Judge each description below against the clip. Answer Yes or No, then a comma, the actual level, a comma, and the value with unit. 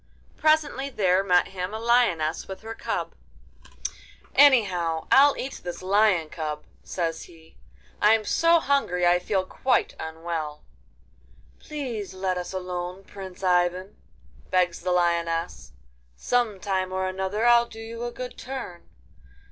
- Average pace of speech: No, slow, 130 wpm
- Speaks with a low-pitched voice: No, high, 190 Hz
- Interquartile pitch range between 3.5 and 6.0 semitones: Yes, average, 4.6 semitones